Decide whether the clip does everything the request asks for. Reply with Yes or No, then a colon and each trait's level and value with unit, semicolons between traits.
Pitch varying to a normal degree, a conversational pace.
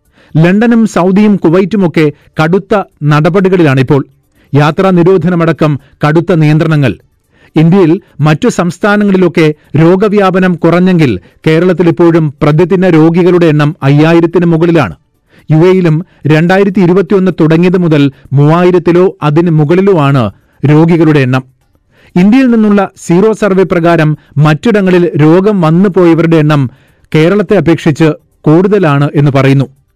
Yes: average, 3.6 semitones; average, 90 wpm